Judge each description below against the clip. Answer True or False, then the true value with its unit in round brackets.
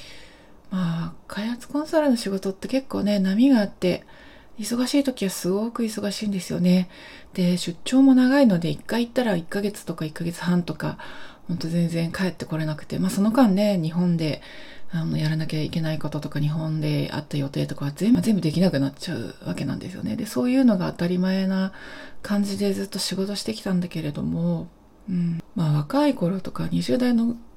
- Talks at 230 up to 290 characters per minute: False (375 characters per minute)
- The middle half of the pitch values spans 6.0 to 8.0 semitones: False (5.1 semitones)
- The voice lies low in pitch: False (190 Hz)